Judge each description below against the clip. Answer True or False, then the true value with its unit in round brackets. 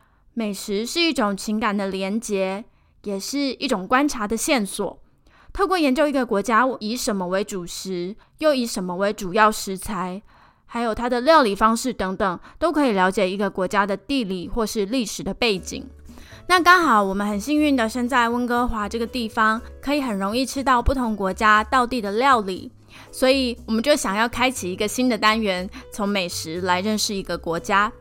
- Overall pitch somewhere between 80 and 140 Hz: False (220 Hz)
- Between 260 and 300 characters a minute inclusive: True (280 characters per minute)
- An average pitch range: True (4.3 semitones)